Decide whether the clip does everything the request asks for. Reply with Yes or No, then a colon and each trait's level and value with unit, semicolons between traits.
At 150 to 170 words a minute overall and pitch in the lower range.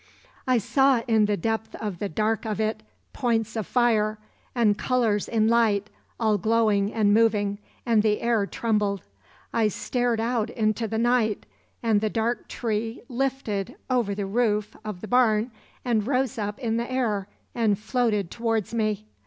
No: average, 160 wpm; high, 220 Hz